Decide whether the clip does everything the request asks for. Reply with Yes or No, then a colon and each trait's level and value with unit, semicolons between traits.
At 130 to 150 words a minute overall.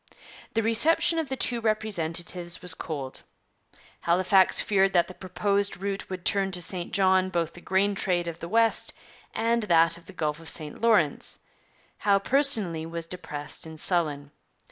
No: average, 165 wpm